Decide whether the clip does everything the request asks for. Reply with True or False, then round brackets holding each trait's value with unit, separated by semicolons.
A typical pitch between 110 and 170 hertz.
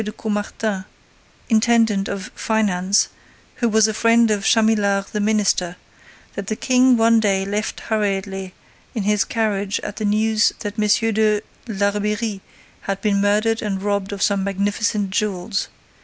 False (210 Hz)